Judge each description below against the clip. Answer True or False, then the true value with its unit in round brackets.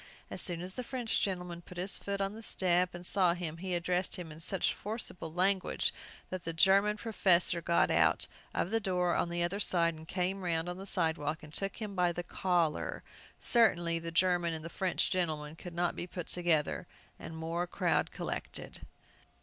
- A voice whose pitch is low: False (175 Hz)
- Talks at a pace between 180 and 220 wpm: True (190 wpm)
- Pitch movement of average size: False (2.2 semitones)